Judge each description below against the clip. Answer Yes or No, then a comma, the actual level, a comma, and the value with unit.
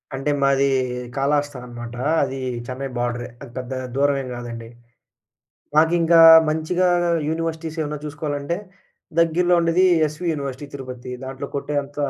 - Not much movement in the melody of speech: No, average, 3.5 semitones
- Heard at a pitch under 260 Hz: Yes, medium, 140 Hz